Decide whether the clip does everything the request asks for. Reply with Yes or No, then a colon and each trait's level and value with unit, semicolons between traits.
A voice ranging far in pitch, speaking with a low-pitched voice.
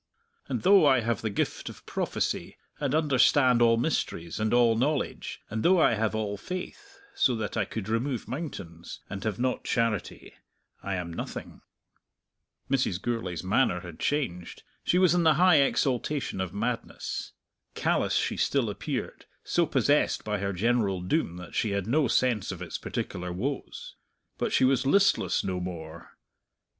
Yes: wide, 6.3 semitones; low, 115 Hz